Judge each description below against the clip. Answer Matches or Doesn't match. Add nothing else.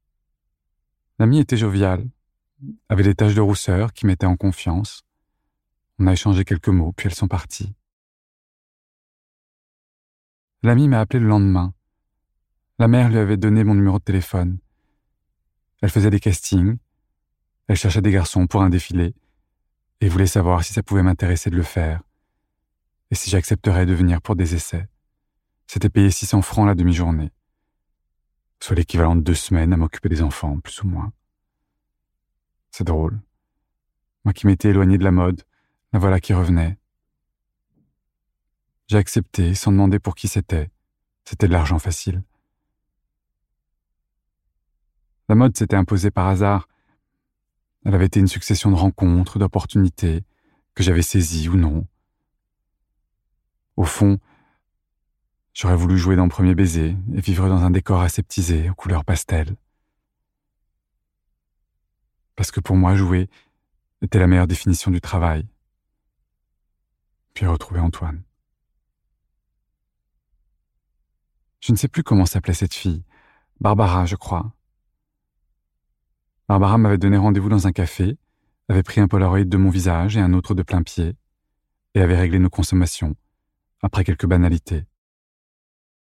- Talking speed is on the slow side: Matches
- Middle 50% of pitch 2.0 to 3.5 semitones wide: Matches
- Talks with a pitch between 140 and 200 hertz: Doesn't match